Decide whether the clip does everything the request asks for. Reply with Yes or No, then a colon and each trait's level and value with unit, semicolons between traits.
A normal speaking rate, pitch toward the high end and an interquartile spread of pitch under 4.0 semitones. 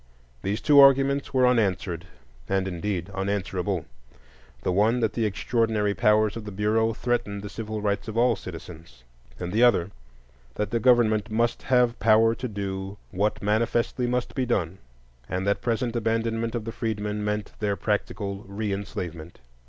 No: average, 155 wpm; low, 105 Hz; average, 2.9 semitones